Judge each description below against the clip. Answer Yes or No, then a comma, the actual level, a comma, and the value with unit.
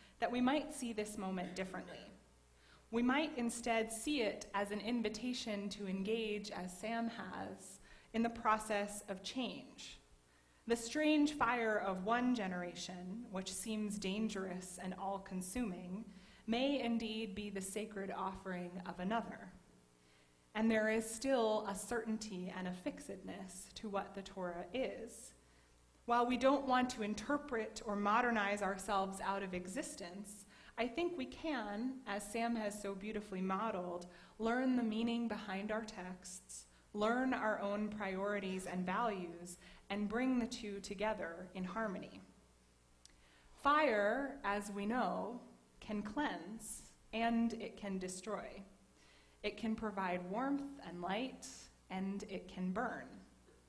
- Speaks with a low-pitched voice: No, high, 205 Hz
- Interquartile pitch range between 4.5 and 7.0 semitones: No, average, 3.6 semitones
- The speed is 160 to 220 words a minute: No, slow, 135 wpm